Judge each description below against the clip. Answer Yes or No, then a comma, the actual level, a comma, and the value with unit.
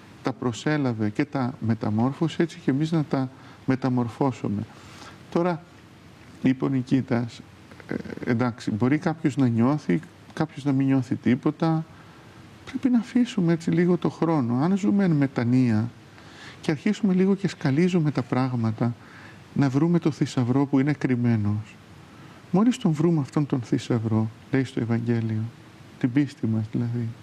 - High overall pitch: No, low, 135 Hz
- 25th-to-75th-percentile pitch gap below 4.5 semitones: No, average, 5.1 semitones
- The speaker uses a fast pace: No, average, 140 wpm